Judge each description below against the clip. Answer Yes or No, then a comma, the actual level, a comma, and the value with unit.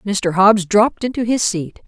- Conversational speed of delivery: Yes, average, 190 wpm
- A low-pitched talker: No, high, 205 Hz